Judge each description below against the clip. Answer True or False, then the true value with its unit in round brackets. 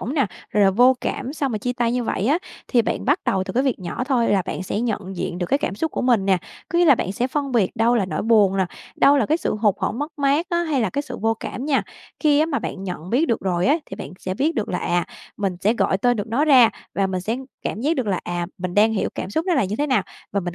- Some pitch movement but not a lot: False (6.2 semitones)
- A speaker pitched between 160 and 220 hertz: False (230 Hz)